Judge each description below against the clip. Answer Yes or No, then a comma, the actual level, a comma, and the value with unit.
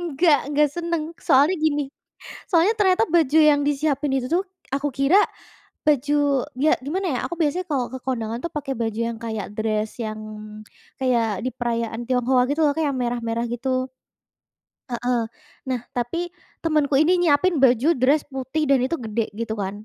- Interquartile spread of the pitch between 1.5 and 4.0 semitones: No, average, 4.5 semitones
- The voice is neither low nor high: No, very high, 275 Hz